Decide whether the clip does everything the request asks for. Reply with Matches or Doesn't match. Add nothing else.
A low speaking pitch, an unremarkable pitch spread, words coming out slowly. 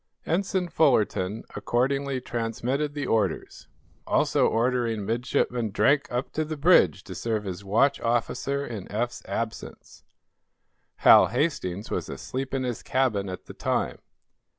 Matches